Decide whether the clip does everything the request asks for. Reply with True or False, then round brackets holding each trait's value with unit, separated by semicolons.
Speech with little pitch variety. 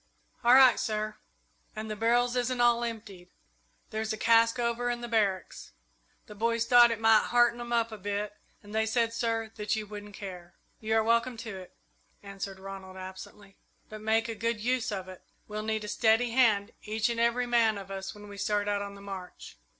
True (2.3 semitones)